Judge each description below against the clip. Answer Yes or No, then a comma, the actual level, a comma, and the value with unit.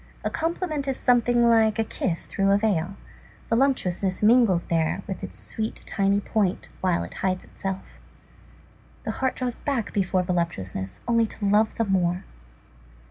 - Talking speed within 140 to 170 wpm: Yes, average, 150 wpm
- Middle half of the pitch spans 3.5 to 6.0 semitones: Yes, average, 4.2 semitones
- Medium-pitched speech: No, high, 205 Hz